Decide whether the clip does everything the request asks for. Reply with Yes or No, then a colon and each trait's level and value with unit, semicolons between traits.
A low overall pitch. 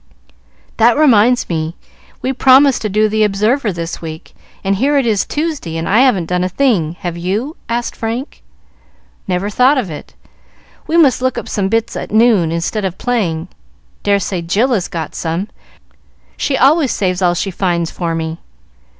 No: high, 205 Hz